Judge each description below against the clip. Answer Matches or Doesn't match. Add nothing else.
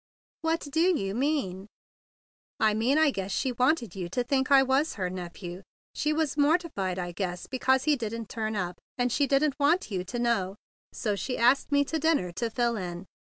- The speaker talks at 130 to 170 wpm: Doesn't match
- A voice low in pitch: Doesn't match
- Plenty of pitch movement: Matches